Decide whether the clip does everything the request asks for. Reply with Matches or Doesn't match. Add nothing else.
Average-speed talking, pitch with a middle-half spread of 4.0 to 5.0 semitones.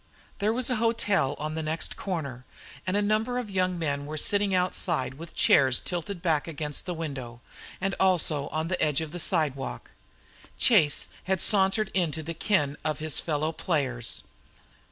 Matches